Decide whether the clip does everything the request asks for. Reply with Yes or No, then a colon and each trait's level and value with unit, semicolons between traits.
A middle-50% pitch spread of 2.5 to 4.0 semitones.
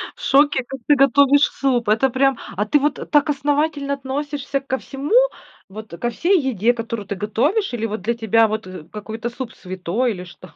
No: average, 4.5 semitones